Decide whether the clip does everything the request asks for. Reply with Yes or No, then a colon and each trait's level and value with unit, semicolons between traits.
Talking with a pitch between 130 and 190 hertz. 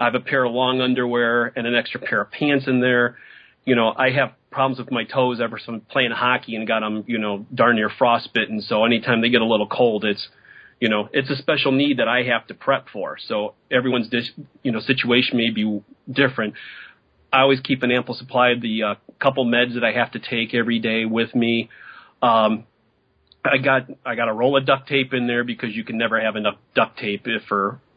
No: low, 120 Hz